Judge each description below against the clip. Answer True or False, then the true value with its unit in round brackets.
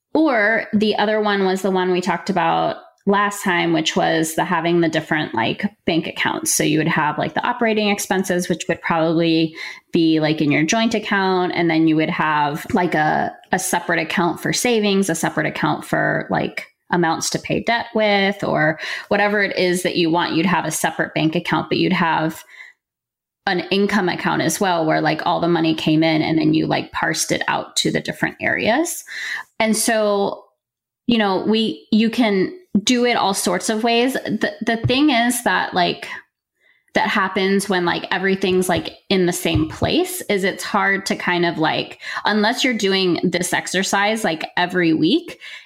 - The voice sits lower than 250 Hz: True (190 Hz)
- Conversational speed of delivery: True (190 wpm)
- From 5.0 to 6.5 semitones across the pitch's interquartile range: False (4.0 semitones)